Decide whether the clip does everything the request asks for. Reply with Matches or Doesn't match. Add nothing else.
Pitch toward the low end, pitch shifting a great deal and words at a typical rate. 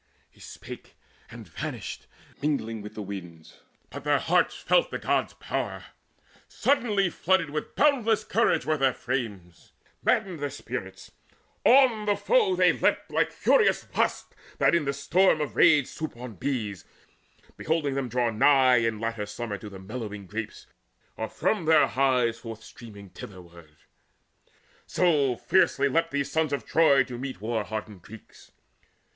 Matches